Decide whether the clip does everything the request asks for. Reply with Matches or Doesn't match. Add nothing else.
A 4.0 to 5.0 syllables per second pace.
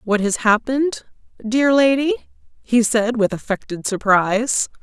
Matches